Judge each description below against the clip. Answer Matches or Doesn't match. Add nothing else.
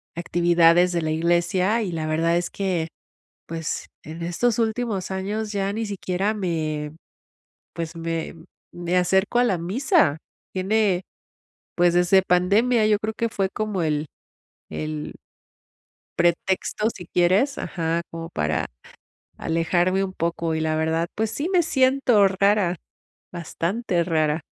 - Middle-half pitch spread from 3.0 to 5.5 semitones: Matches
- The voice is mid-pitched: Matches